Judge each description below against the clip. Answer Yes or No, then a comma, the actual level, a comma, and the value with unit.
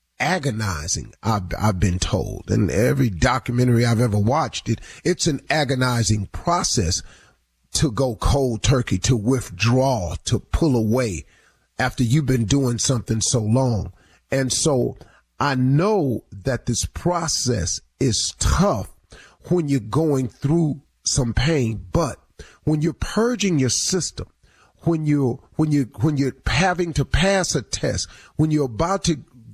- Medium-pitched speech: No, low, 130 Hz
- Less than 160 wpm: Yes, average, 140 wpm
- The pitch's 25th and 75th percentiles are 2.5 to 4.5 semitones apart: No, wide, 5.6 semitones